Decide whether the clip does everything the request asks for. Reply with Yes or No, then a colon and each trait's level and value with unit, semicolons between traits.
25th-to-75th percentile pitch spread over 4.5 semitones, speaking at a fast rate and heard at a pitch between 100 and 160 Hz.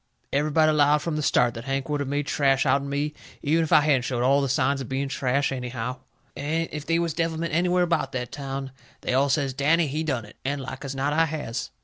No: narrow, 2.5 semitones; fast, 240 wpm; medium, 140 Hz